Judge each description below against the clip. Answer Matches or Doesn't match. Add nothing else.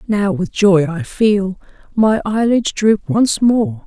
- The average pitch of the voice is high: Matches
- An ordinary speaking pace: Matches